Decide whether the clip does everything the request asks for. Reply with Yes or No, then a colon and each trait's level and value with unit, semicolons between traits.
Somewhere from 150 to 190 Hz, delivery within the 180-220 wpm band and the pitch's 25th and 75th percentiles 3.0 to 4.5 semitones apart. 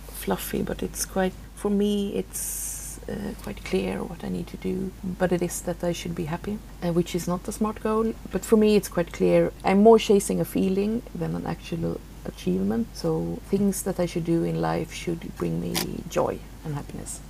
Yes: medium, 185 Hz; fast, 205 wpm; average, 3.3 semitones